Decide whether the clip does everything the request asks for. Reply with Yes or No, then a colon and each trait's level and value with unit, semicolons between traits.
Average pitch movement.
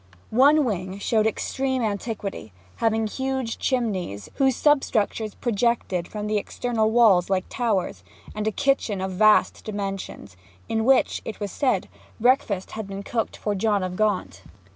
Yes: average, 3.4 semitones